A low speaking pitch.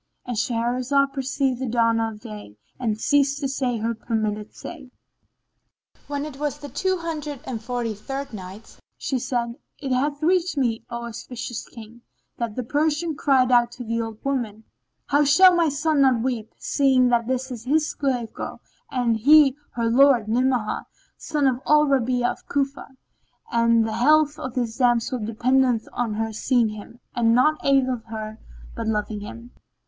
No: very high, 250 Hz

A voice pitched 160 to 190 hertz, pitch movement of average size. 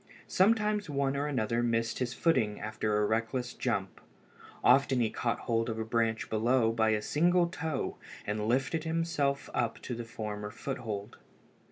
No: low, 120 Hz; average, 4.0 semitones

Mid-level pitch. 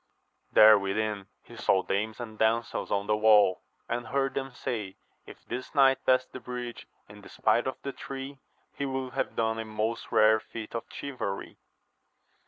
No: low, 115 Hz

